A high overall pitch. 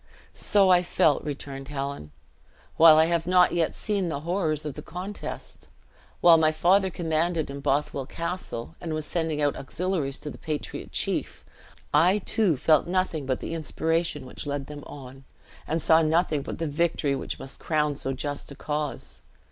No: medium, 155 Hz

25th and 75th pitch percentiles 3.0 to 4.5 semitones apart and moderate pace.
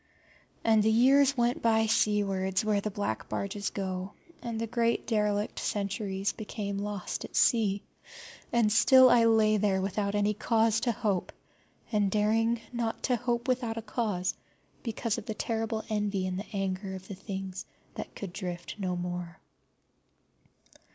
No: narrow, 2.6 semitones; average, 155 wpm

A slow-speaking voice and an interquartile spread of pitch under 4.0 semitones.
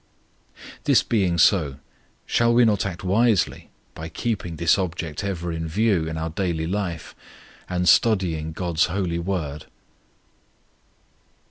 Yes: slow, 130 wpm; average, 3.4 semitones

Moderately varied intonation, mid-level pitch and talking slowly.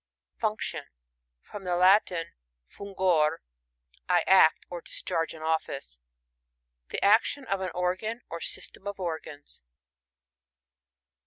Yes: average, 3.5 semitones; medium, 180 Hz; slow, 110 wpm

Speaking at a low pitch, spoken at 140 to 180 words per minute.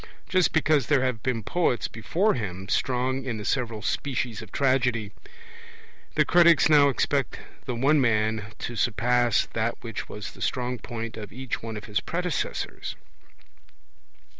Yes: low, 125 Hz; average, 150 wpm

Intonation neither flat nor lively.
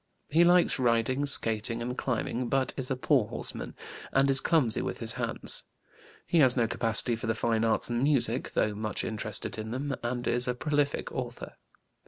Yes: average, 3.1 semitones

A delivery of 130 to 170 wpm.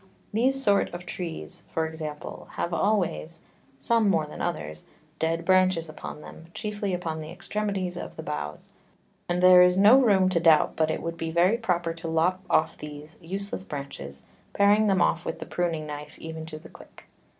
No: average, 185 wpm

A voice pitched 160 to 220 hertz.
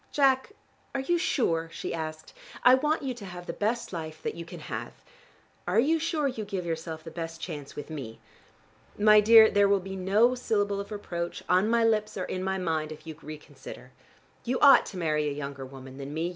Yes: medium, 185 Hz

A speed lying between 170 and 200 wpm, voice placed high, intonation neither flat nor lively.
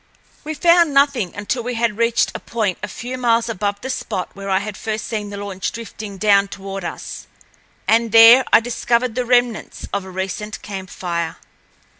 Yes: average, 185 wpm; high, 220 Hz; average, 3.3 semitones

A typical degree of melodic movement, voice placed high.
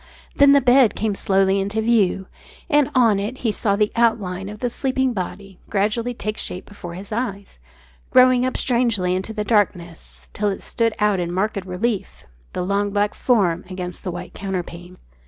Yes: average, 3.7 semitones; high, 205 Hz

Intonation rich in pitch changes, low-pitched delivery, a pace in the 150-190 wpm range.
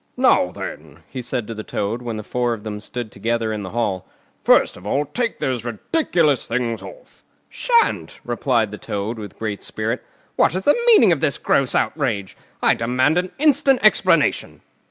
Yes: wide, 6.6 semitones; low, 120 Hz; average, 175 wpm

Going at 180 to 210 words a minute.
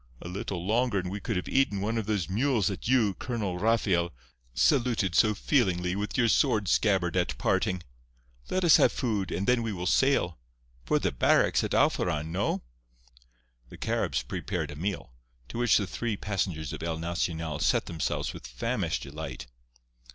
No: average, 170 wpm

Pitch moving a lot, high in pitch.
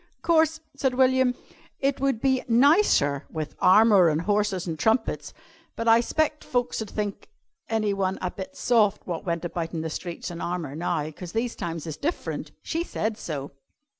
Yes: wide, 6.9 semitones; high, 210 Hz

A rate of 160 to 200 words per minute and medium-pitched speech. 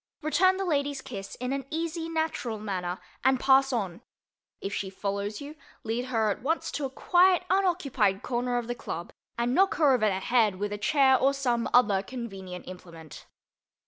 No: average, 180 wpm; high, 245 Hz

